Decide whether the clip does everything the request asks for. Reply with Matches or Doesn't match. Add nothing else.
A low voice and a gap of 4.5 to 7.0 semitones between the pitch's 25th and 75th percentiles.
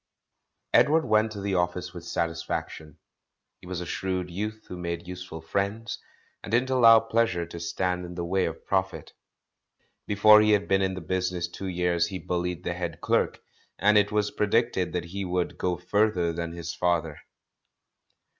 Doesn't match